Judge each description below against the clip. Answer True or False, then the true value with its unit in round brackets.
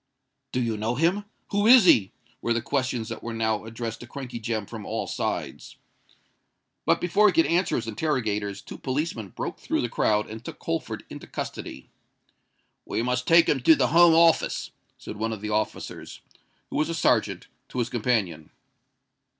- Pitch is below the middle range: True (120 Hz)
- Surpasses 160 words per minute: True (180 wpm)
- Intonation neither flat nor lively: False (6.6 semitones)